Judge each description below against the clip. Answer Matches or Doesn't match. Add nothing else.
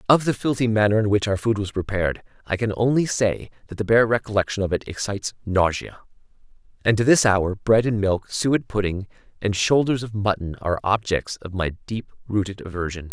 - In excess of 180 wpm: Matches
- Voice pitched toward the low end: Matches